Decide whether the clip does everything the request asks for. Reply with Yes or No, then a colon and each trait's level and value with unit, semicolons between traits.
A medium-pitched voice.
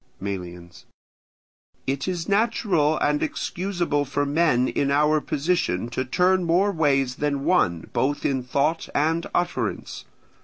Yes: medium, 145 Hz